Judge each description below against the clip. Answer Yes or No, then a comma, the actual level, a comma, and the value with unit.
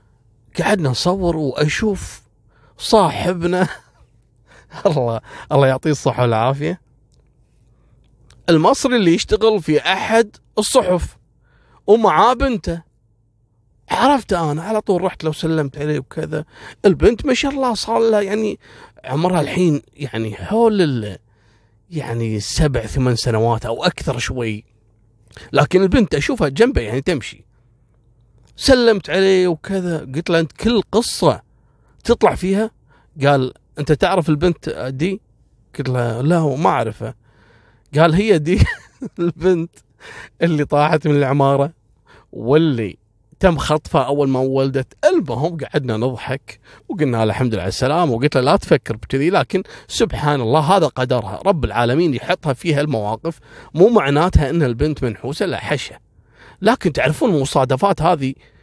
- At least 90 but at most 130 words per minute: Yes, average, 125 wpm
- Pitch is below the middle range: No, medium, 145 Hz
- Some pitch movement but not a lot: No, wide, 7.1 semitones